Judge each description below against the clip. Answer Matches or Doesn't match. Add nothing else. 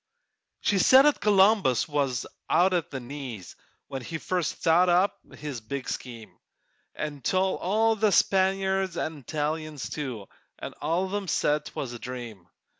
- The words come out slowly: Doesn't match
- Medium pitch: Matches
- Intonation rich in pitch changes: Matches